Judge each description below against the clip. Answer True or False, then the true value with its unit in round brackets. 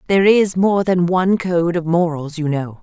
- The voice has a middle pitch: True (175 Hz)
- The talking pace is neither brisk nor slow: False (210 wpm)